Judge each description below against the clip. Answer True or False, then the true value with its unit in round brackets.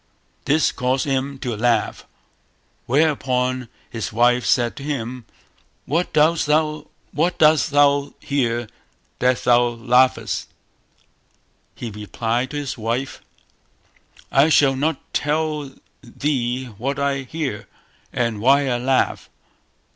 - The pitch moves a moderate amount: True (3.1 semitones)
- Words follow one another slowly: True (105 wpm)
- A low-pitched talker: True (130 Hz)